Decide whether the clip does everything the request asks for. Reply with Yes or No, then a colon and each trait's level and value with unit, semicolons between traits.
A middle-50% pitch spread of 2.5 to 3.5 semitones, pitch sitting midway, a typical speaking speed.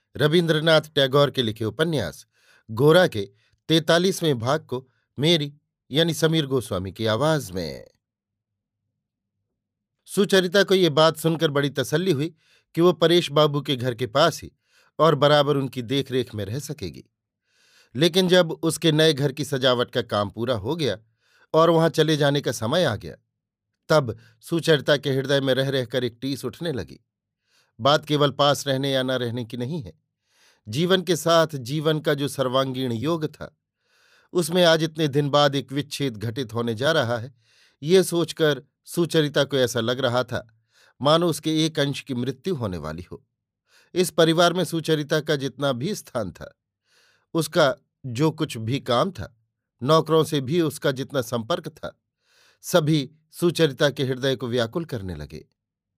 No: average, 4.5 semitones; medium, 145 Hz; average, 160 wpm